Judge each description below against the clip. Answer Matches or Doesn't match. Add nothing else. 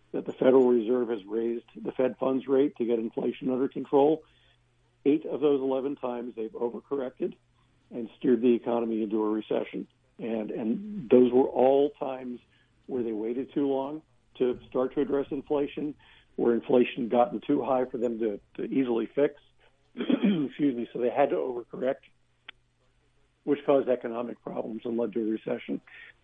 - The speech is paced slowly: Doesn't match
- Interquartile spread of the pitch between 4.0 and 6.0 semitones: Doesn't match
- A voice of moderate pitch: Doesn't match